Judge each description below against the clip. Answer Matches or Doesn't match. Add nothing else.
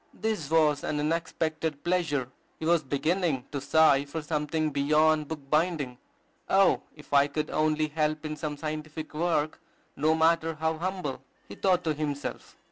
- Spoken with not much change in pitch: Matches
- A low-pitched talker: Doesn't match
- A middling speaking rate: Matches